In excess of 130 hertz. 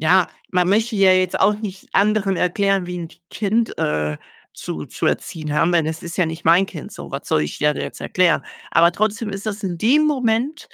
Yes: medium, 185 Hz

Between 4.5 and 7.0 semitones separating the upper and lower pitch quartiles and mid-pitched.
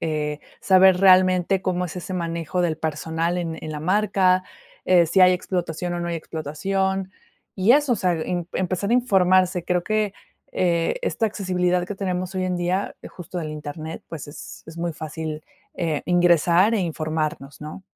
No: narrow, 2.5 semitones; medium, 180 Hz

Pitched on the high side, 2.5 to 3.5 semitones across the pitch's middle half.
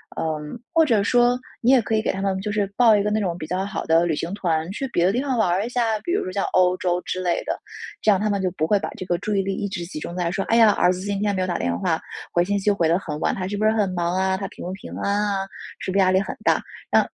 Yes: high, 195 Hz; average, 2.9 semitones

